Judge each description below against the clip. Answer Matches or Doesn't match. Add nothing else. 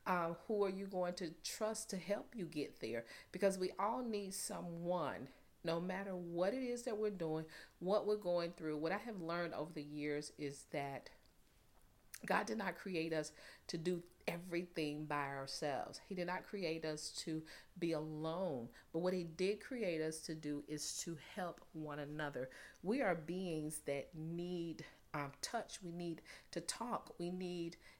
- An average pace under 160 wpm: Doesn't match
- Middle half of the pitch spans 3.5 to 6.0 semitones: Doesn't match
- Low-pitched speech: Doesn't match